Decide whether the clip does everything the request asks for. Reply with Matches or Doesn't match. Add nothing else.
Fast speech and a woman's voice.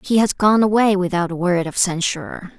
Matches